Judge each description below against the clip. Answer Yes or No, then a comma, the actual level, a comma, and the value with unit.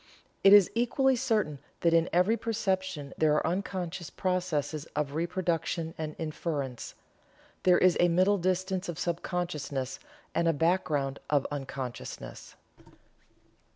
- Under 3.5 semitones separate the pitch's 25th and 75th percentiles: No, average, 3.8 semitones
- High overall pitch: No, medium, 170 Hz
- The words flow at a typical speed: No, slow, 125 wpm